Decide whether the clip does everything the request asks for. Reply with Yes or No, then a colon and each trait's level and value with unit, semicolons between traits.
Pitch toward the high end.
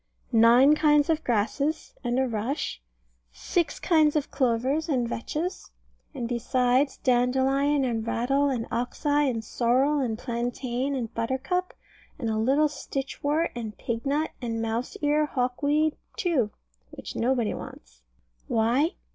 Yes: very high, 260 Hz